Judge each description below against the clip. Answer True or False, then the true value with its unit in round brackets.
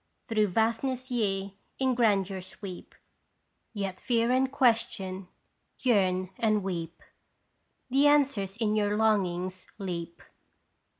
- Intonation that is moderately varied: True (3.9 semitones)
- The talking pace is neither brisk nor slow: False (110 wpm)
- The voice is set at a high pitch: True (205 Hz)